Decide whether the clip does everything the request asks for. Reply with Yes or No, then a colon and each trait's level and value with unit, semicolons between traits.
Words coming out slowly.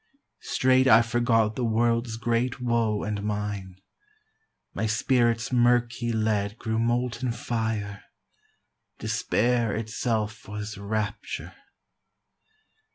Yes: slow, 95 wpm